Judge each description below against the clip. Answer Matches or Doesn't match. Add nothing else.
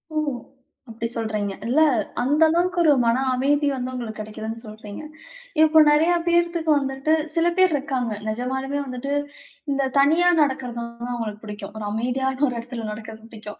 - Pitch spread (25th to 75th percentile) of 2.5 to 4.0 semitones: Doesn't match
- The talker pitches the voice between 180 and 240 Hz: Doesn't match